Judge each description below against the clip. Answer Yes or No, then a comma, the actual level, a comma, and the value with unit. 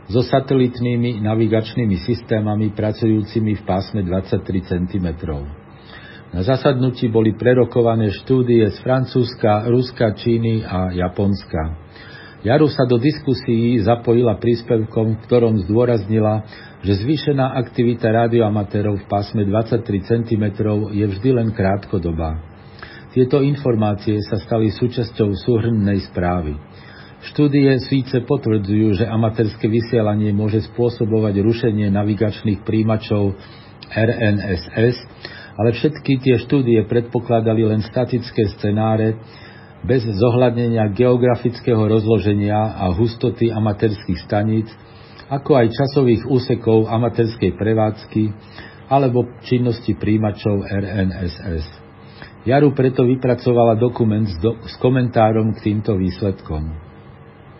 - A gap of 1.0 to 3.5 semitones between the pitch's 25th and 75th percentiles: Yes, narrow, 2.6 semitones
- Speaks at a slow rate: Yes, slow, 100 wpm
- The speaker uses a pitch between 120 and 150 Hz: No, low, 110 Hz